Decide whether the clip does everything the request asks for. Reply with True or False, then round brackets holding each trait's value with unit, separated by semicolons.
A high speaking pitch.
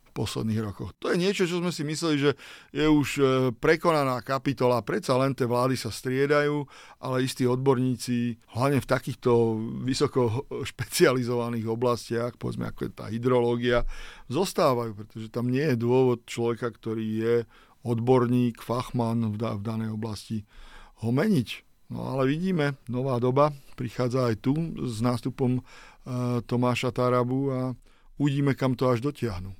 False (125 Hz)